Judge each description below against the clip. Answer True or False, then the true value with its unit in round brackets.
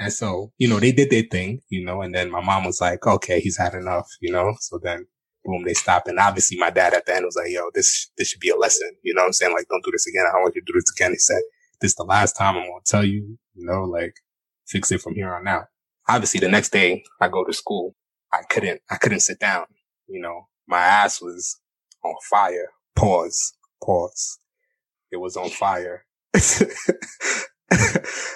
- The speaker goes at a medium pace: False (230 wpm)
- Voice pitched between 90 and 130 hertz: False (140 Hz)